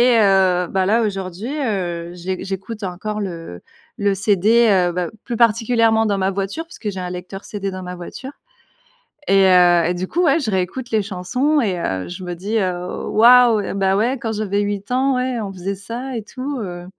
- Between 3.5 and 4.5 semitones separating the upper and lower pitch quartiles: Yes, average, 4.0 semitones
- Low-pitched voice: No, high, 200 Hz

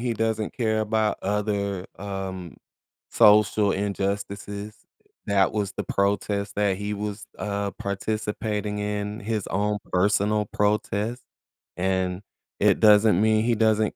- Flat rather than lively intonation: Yes, narrow, 1.2 semitones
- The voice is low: Yes, low, 105 Hz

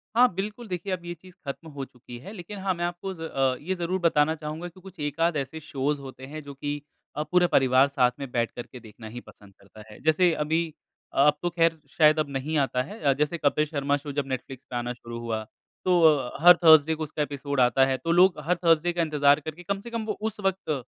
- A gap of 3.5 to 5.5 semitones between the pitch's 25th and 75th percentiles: Yes, average, 4.3 semitones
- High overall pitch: No, medium, 150 Hz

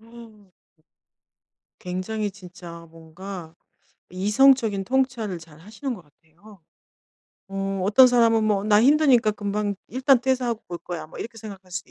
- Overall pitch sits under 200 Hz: No, high, 205 Hz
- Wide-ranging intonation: No, average, 4.2 semitones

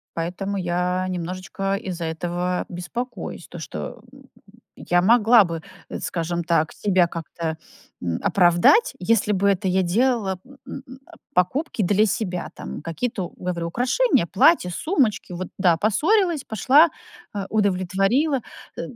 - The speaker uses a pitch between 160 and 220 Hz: Yes, high, 190 Hz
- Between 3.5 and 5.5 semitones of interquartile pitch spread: Yes, average, 4.6 semitones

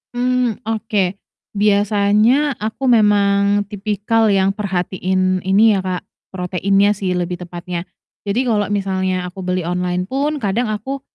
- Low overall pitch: No, high, 200 Hz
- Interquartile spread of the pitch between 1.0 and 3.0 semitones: Yes, average, 2.7 semitones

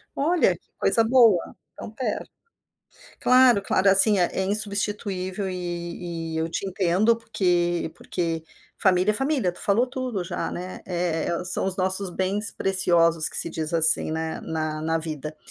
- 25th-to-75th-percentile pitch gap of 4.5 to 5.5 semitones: No, average, 3.7 semitones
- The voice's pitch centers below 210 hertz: Yes, medium, 185 Hz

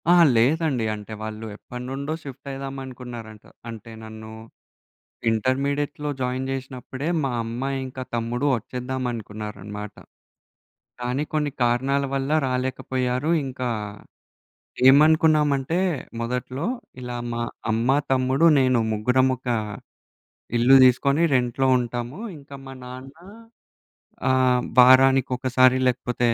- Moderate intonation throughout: No, narrow, 2.0 semitones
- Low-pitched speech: Yes, low, 130 Hz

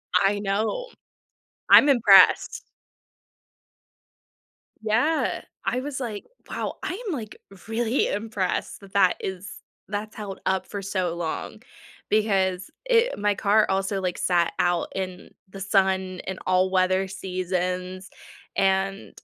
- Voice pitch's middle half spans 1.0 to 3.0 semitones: Yes, narrow, 2.4 semitones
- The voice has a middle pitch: No, high, 195 Hz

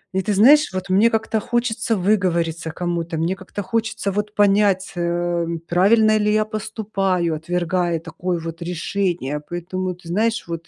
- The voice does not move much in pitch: No, average, 3.5 semitones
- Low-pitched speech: No, medium, 185 Hz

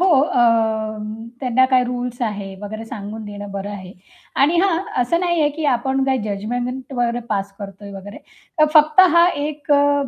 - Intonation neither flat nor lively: No, wide, 5.8 semitones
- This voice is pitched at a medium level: No, high, 245 Hz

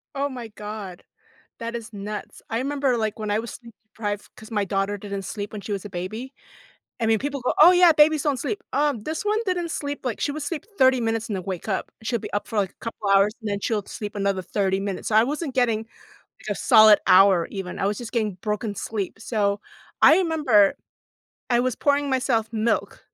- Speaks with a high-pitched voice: Yes, high, 220 Hz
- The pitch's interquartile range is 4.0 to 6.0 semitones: Yes, average, 4.4 semitones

